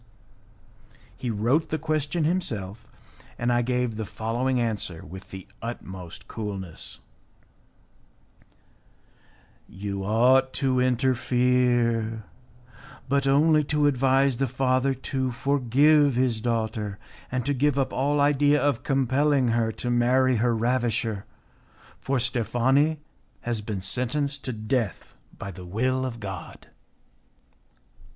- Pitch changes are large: No, average, 3.4 semitones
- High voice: No, low, 125 Hz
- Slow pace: Yes, slow, 115 wpm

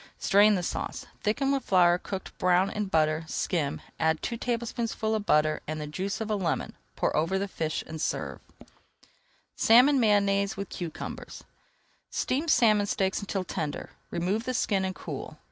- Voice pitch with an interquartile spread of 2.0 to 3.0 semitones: No, average, 4.2 semitones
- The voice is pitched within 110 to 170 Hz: No, high, 195 Hz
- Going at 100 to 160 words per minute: No, average, 170 wpm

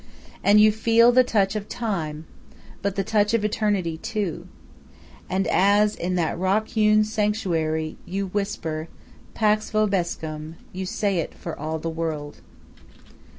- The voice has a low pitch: No, high, 195 Hz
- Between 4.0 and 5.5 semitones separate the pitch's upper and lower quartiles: Yes, average, 4.4 semitones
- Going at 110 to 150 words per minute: Yes, average, 140 wpm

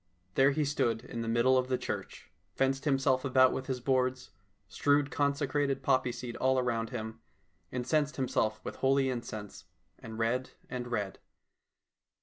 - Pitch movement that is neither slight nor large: No, narrow, 2.3 semitones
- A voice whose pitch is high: No, low, 130 Hz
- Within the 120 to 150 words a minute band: Yes, average, 145 wpm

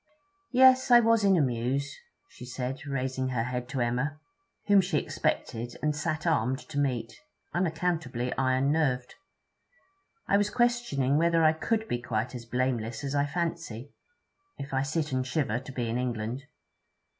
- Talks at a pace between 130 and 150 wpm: No, average, 160 wpm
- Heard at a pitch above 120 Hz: Yes, low, 135 Hz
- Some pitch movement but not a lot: Yes, average, 4.5 semitones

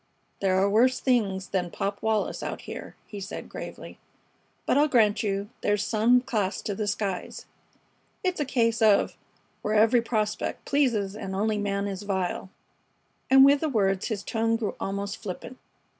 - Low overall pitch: No, high, 210 Hz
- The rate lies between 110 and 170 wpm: Yes, average, 165 wpm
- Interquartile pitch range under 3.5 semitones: Yes, average, 2.8 semitones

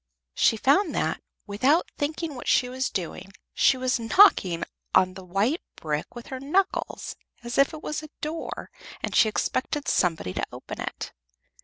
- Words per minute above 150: Yes, average, 165 wpm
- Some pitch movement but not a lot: No, wide, 7.4 semitones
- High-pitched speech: Yes, very high, 255 Hz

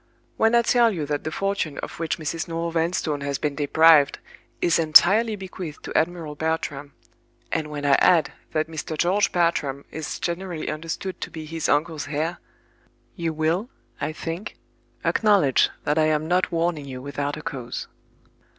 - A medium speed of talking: Yes, average, 160 wpm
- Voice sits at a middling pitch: Yes, medium, 160 Hz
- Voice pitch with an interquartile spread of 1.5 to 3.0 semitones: Yes, average, 2.7 semitones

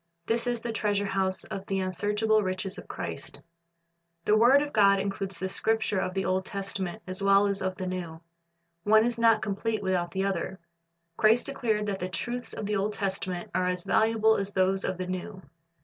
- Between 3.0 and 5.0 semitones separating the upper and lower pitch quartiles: No, narrow, 2.5 semitones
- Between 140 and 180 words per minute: No, average, 195 wpm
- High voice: Yes, high, 195 Hz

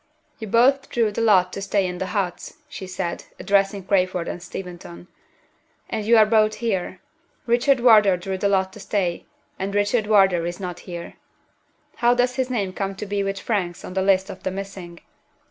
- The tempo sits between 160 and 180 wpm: No, average, 190 wpm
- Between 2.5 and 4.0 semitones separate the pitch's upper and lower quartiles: Yes, average, 2.9 semitones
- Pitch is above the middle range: Yes, high, 195 Hz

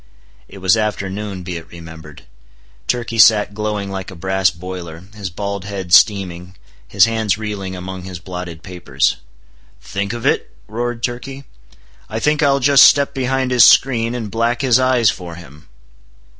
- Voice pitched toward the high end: No, low, 100 Hz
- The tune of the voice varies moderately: Yes, average, 4.4 semitones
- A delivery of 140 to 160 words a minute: Yes, average, 155 wpm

